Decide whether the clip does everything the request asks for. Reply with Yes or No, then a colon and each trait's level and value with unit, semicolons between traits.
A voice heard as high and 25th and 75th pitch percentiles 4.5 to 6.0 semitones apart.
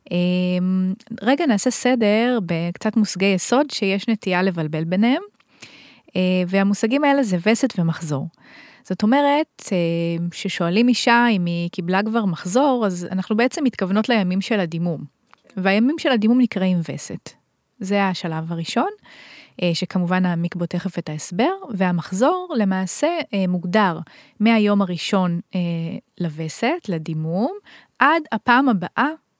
Yes: high, 195 Hz; average, 5.2 semitones